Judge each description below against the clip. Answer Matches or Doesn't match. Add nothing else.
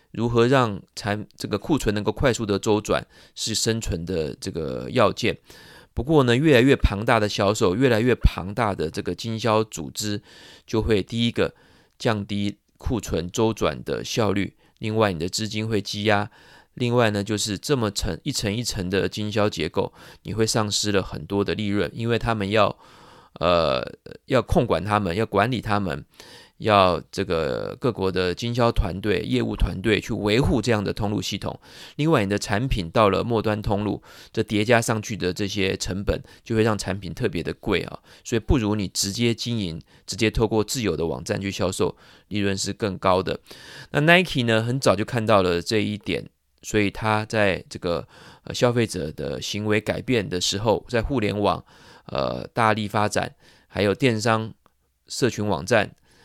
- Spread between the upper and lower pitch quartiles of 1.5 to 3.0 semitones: Matches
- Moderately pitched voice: Doesn't match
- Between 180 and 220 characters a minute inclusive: Doesn't match